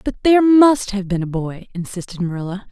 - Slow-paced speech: No, average, 200 wpm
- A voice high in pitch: Yes, high, 210 Hz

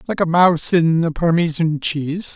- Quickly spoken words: No, average, 180 wpm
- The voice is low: No, medium, 165 Hz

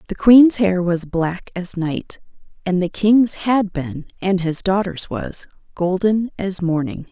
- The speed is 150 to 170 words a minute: Yes, average, 160 wpm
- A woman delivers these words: Yes, female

